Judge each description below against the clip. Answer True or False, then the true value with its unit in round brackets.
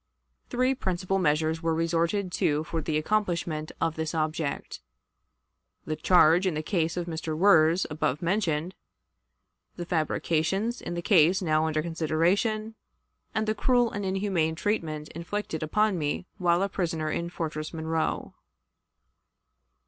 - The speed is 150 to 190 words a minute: False (135 wpm)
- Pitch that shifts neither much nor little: True (3.4 semitones)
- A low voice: False (165 Hz)